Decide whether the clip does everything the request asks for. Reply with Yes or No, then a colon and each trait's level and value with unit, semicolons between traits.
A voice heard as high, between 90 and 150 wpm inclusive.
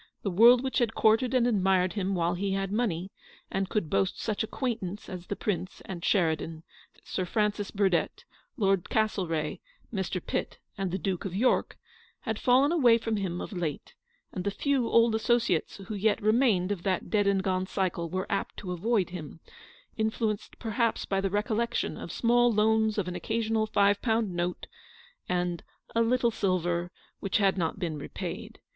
No: high, 200 Hz; average, 175 wpm